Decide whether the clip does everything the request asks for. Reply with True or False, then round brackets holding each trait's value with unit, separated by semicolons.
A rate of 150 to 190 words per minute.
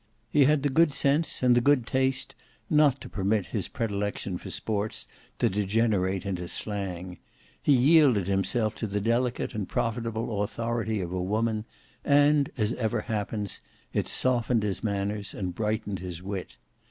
True (155 wpm)